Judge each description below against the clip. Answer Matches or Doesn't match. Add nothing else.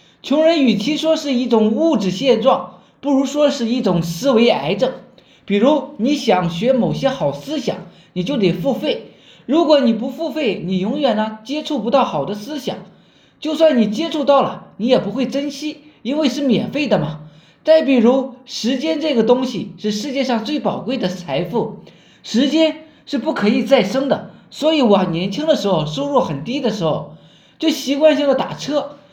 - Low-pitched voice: Doesn't match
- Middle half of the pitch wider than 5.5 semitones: Matches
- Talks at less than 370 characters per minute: Matches